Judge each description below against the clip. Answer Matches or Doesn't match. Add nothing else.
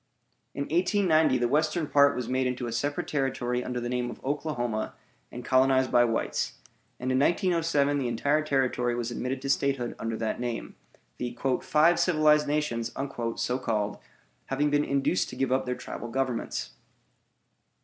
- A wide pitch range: Doesn't match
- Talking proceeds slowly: Doesn't match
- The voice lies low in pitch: Matches